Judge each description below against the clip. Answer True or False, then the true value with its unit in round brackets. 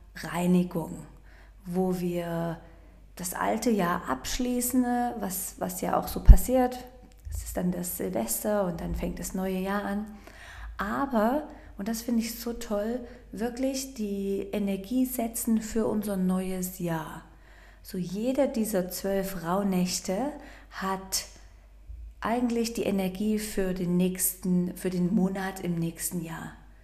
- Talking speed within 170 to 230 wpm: False (130 wpm)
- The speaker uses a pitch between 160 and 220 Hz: True (190 Hz)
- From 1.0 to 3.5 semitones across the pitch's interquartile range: False (4.4 semitones)